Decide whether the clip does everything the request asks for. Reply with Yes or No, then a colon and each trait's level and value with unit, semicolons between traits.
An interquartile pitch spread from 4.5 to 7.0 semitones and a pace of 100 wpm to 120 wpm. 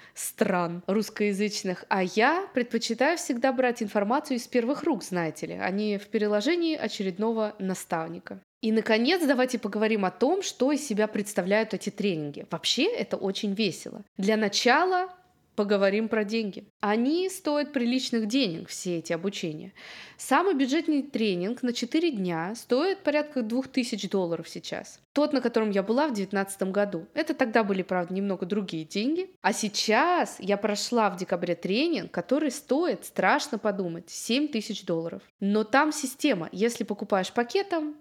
No: wide, 5.4 semitones; average, 145 wpm